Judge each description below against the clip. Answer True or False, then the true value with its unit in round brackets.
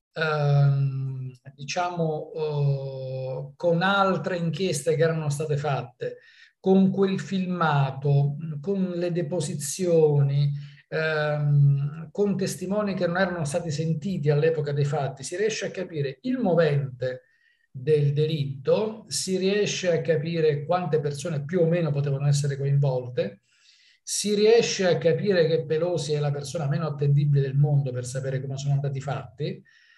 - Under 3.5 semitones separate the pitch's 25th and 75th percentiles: False (4.1 semitones)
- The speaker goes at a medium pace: True (130 wpm)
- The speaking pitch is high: False (155 Hz)